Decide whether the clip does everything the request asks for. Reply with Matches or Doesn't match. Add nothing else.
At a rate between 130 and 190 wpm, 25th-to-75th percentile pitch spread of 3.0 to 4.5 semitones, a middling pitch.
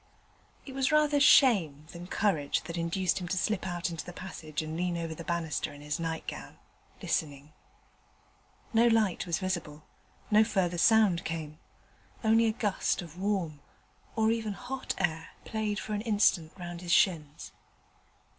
Doesn't match